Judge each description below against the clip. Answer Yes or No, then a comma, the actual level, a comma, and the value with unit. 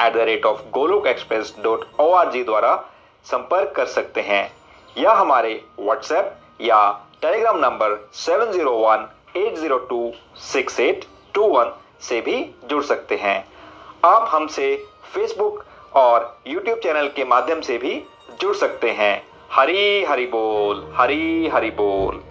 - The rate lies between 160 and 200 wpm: No, average, 145 wpm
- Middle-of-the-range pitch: No, high, 230 Hz